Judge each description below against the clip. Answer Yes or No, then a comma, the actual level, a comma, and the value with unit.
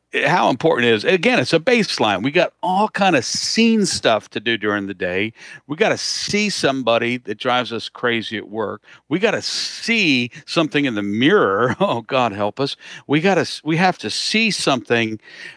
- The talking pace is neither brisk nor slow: Yes, average, 195 wpm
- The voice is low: Yes, low, 125 Hz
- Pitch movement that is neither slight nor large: No, wide, 6.7 semitones